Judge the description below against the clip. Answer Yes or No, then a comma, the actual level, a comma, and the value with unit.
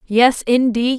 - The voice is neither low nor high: No, high, 240 Hz